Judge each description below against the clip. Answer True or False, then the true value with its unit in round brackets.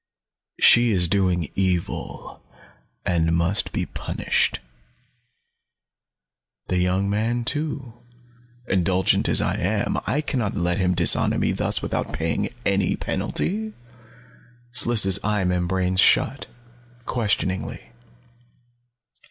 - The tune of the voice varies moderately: True (3.9 semitones)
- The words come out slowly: True (105 wpm)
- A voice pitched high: False (95 Hz)